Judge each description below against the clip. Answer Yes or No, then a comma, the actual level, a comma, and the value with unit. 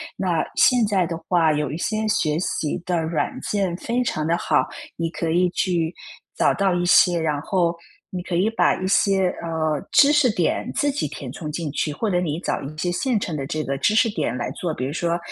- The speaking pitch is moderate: Yes, medium, 175 Hz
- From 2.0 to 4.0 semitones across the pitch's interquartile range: Yes, average, 3.7 semitones